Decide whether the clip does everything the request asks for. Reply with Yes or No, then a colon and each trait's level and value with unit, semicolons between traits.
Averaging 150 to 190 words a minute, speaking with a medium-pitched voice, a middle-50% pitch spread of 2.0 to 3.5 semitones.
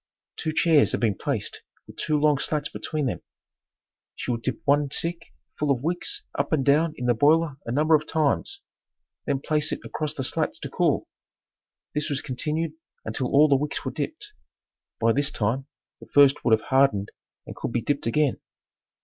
Yes: average, 185 wpm; medium, 145 Hz; average, 2.9 semitones